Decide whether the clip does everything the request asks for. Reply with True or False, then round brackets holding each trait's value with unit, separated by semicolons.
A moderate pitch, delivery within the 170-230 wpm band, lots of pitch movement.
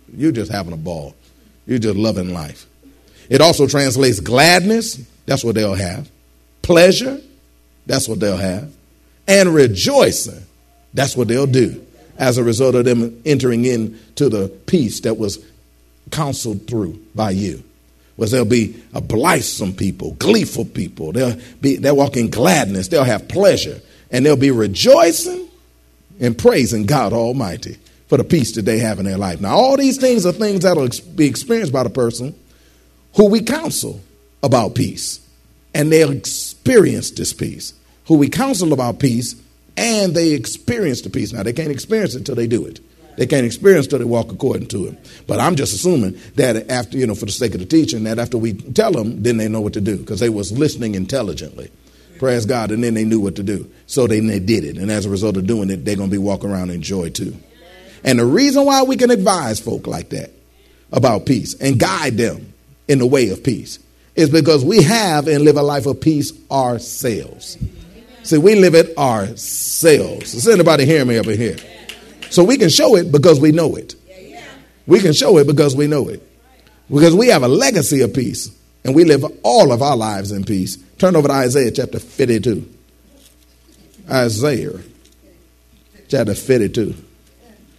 False (120 Hz; 190 wpm; 6.7 semitones)